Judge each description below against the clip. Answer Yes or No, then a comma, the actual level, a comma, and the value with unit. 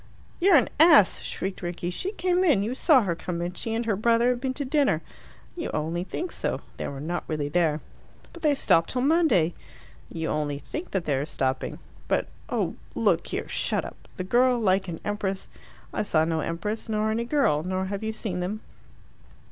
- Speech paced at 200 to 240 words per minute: Yes, fast, 205 wpm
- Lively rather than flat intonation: Yes, wide, 7.0 semitones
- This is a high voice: Yes, high, 200 Hz